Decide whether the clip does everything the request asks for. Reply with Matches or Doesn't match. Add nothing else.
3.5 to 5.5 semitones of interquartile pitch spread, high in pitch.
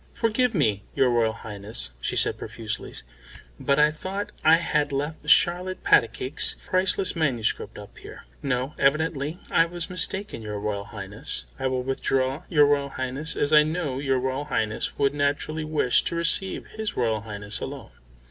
Doesn't match